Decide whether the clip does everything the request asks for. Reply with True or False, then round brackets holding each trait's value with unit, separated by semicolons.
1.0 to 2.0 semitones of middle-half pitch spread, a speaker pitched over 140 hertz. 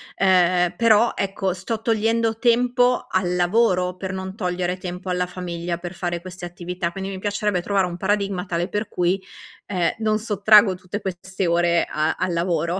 False (2.7 semitones; 185 Hz)